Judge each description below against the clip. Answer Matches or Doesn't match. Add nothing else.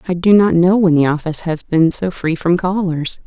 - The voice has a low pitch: Doesn't match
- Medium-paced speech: Doesn't match